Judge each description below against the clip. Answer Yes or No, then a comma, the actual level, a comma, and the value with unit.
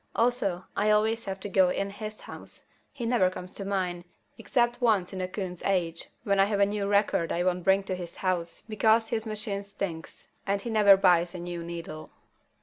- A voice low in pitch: No, high, 195 Hz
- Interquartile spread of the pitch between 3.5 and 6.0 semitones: No, average, 2.9 semitones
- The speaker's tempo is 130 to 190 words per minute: No, fast, 205 wpm